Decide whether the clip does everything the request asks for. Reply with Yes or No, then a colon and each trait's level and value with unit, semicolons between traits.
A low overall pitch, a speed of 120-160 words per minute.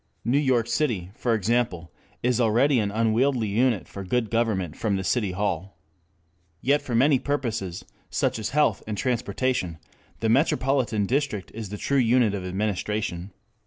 Yes: low, 115 Hz; average, 155 wpm